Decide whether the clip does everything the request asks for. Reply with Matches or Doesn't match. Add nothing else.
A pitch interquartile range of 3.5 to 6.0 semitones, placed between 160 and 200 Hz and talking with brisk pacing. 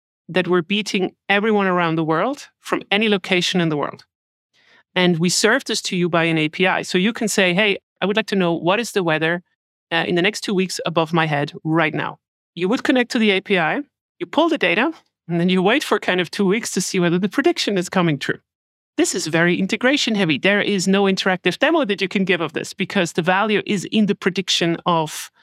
Doesn't match